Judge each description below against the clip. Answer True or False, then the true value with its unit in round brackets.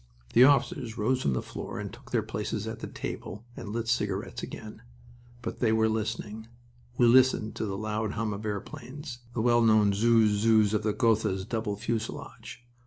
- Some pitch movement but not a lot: False (1.9 semitones)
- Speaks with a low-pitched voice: True (110 Hz)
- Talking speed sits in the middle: True (180 wpm)